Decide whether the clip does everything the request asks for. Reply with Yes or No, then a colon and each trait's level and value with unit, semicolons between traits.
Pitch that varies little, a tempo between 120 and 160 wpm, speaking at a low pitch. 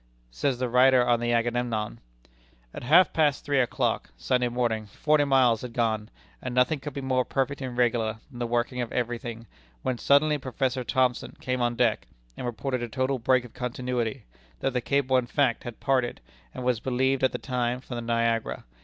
No: narrow, 1.8 semitones; average, 200 wpm; low, 125 Hz